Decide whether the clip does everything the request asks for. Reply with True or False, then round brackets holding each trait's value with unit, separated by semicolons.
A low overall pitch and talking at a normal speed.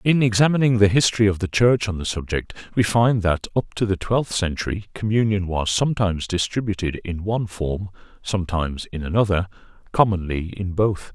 True (100 Hz; 165 wpm)